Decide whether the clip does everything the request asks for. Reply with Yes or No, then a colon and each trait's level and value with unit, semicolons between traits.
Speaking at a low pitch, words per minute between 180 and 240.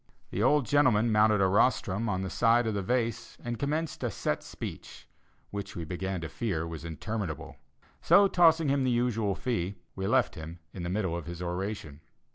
Yes: low, 105 Hz; average, 190 wpm